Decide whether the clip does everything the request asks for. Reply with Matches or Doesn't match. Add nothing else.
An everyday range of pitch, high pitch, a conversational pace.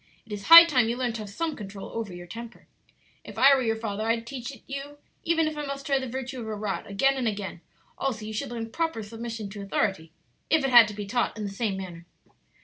Doesn't match